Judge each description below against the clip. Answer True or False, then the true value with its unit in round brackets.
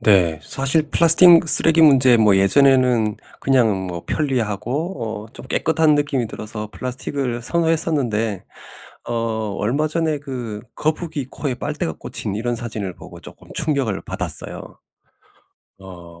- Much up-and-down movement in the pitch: True (6.1 semitones)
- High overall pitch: False (125 Hz)